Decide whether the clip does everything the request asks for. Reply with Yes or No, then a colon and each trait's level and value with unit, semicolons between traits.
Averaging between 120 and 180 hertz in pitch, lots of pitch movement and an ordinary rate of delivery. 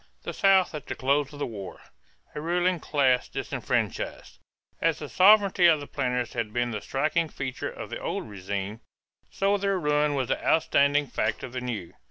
Yes: medium, 140 Hz; wide, 5.7 semitones; average, 185 wpm